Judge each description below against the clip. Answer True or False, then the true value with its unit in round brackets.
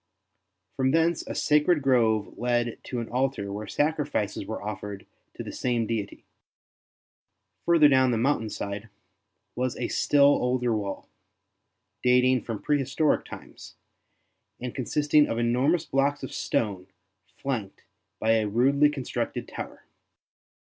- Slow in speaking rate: True (125 wpm)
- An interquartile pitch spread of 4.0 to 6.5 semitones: True (4.4 semitones)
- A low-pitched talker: True (125 Hz)